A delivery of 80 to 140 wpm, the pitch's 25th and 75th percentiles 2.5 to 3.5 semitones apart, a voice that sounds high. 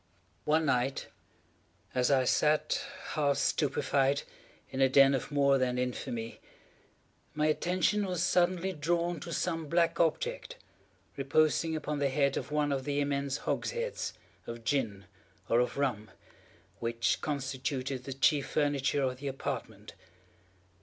No: slow, 135 wpm; average, 2.9 semitones; medium, 140 Hz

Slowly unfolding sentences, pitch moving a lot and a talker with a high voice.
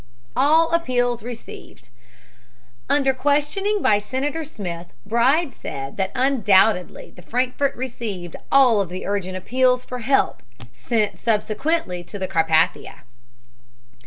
Yes: slow, 115 wpm; wide, 6.3 semitones; high, 235 Hz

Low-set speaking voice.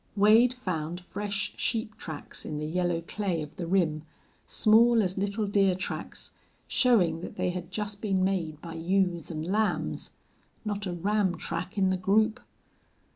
No: high, 190 Hz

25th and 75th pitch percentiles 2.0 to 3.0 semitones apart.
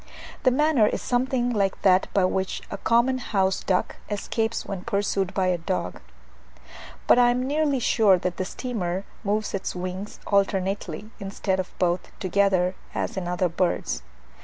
No: average, 3.9 semitones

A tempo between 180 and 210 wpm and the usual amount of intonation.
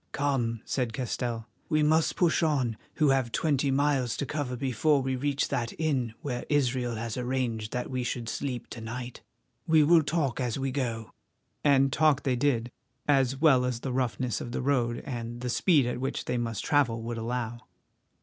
Yes: average, 185 wpm; average, 3.0 semitones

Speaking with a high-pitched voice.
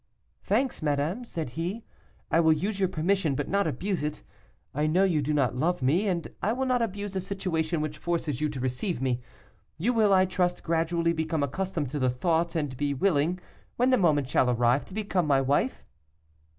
No: medium, 165 Hz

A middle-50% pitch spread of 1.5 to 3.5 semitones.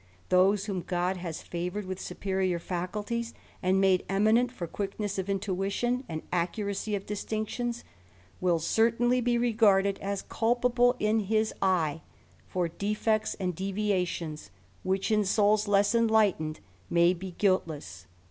Yes: average, 3.2 semitones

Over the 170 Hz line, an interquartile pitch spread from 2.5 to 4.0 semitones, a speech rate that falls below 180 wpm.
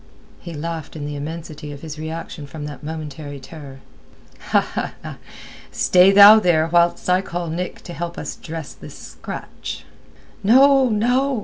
No: medium, 165 Hz; average, 3.3 semitones; average, 140 wpm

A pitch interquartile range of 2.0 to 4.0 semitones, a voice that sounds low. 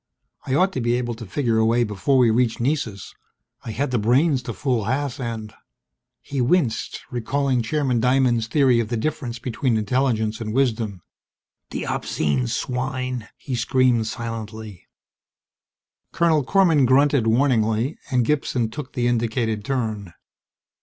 Yes: average, 3.2 semitones; low, 120 Hz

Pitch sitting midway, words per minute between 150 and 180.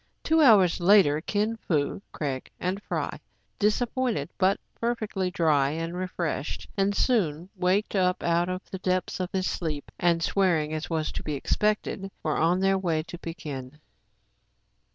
Yes: medium, 180 Hz; average, 155 wpm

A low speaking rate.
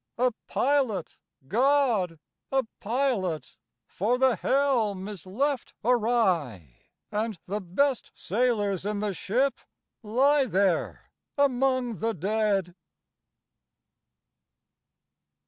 Yes: slow, 90 wpm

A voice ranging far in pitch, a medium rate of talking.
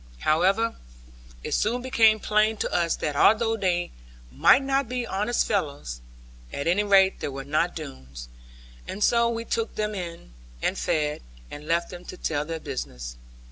Yes: wide, 6.8 semitones; average, 165 wpm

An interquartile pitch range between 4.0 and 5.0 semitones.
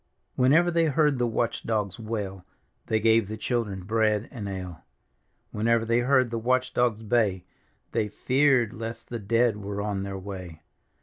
No: average, 3.1 semitones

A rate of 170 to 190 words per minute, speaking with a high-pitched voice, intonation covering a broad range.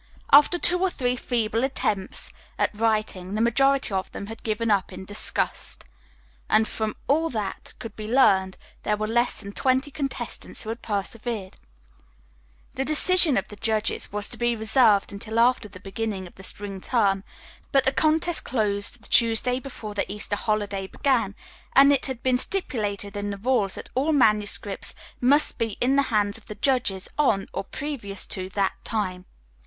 No: average, 175 wpm; high, 220 Hz; average, 4.3 semitones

